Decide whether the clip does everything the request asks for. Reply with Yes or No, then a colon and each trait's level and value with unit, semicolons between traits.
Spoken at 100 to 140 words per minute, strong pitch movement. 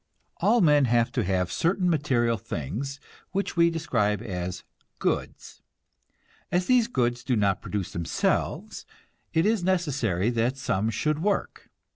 Yes: slow, 135 wpm; wide, 8.3 semitones